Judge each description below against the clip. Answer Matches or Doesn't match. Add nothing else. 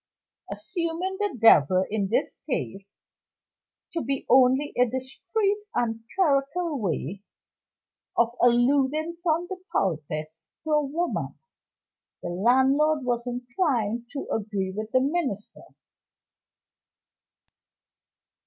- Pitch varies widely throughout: Matches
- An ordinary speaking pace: Doesn't match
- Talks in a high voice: Matches